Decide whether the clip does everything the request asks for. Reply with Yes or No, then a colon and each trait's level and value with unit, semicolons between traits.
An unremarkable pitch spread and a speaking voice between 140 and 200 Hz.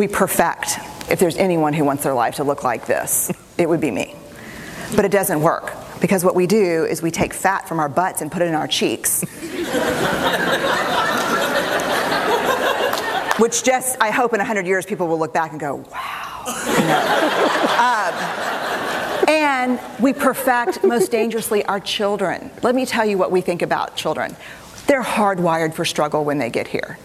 No: wide, 5.7 semitones; high, 190 Hz